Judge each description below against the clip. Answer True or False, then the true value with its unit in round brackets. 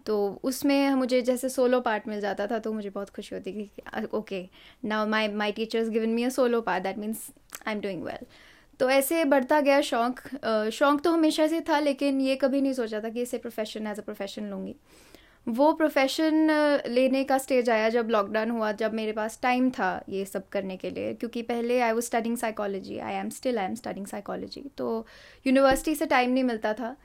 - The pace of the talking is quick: True (210 wpm)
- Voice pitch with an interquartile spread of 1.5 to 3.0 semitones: False (3.9 semitones)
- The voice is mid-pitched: False (235 Hz)